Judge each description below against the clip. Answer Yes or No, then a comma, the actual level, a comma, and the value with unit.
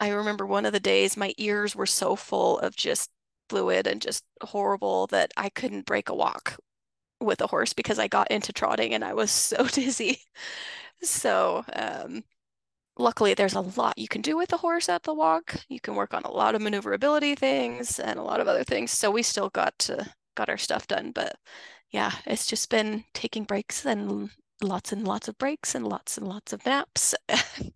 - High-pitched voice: Yes, high, 220 Hz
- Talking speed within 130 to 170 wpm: No, fast, 205 wpm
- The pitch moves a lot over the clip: Yes, wide, 6.5 semitones